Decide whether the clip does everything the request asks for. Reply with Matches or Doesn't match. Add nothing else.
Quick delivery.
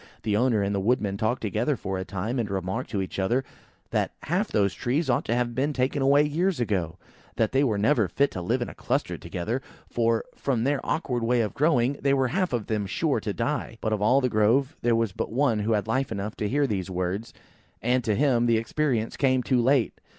Matches